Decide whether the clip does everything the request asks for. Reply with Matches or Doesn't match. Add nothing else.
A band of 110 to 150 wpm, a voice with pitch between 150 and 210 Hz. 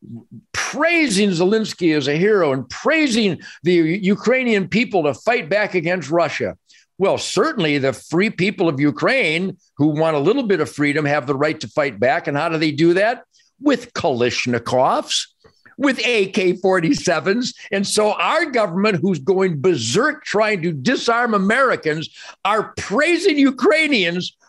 Matches